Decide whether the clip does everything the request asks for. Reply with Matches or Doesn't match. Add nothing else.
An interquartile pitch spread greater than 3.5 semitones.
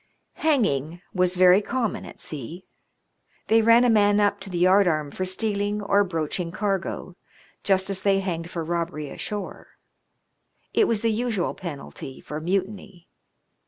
Doesn't match